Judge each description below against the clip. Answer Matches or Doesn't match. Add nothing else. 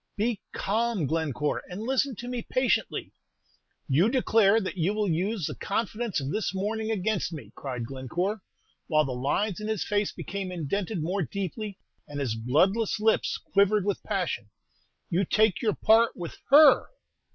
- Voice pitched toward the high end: Matches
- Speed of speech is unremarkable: Matches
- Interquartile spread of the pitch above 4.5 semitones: Matches